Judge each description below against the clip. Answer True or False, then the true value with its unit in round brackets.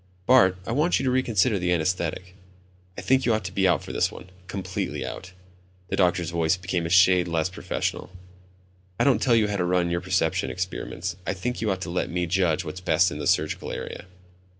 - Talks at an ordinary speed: False (215 wpm)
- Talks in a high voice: False (90 Hz)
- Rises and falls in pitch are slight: True (2.2 semitones)